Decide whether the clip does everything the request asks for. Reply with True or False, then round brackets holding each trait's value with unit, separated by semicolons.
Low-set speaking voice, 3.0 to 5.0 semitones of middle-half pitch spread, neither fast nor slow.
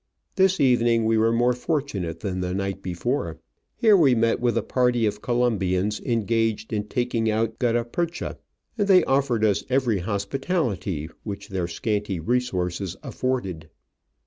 True (115 Hz; 4.1 semitones; 150 wpm)